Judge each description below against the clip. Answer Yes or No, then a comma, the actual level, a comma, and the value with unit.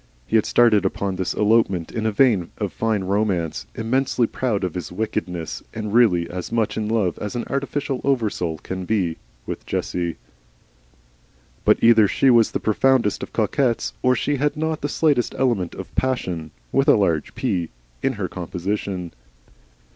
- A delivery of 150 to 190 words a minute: Yes, average, 165 wpm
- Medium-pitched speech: No, low, 105 Hz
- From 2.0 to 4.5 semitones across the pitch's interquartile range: No, average, 5.1 semitones